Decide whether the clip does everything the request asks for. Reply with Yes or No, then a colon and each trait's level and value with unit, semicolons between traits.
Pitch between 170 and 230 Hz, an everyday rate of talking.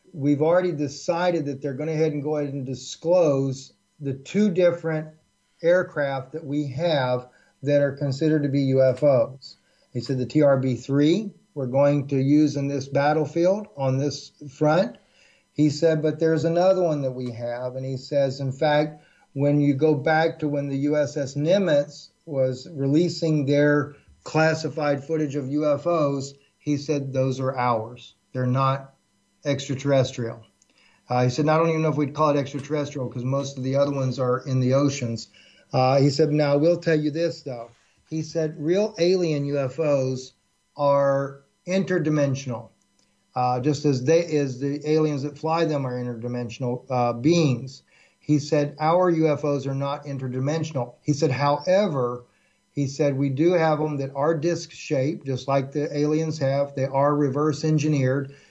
No: medium, 145 Hz; average, 170 wpm